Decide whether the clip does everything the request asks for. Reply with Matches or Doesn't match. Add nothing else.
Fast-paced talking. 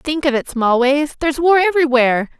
Doesn't match